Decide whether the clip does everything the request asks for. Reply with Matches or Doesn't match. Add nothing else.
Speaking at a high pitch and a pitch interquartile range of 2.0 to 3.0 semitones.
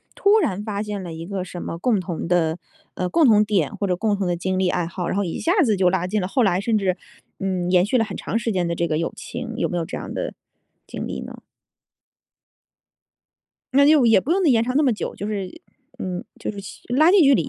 Doesn't match